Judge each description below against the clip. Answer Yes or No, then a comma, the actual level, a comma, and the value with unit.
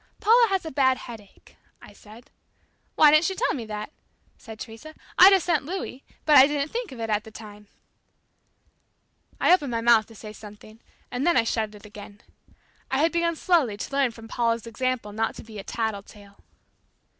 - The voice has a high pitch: Yes, high, 235 Hz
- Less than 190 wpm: No, average, 195 wpm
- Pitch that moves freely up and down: Yes, wide, 6.1 semitones